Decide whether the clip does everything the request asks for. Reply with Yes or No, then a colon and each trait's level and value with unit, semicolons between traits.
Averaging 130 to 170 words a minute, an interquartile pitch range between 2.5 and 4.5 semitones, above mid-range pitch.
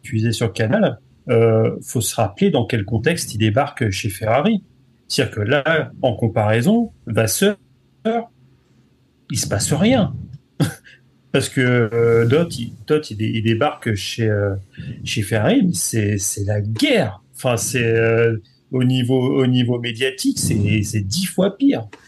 No: average, 150 wpm; average, 3.7 semitones; low, 120 Hz